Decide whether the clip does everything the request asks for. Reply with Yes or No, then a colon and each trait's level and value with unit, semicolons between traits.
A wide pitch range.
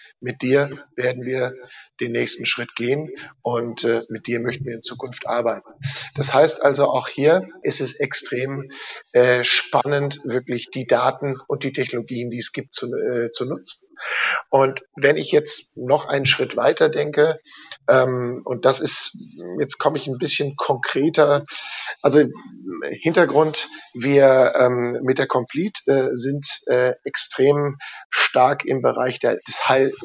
No: narrow, 2.5 semitones